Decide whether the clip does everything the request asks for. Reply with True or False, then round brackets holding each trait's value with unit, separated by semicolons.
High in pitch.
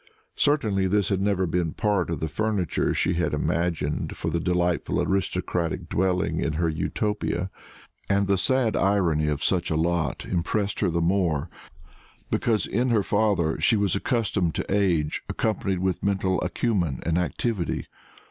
False (90 Hz)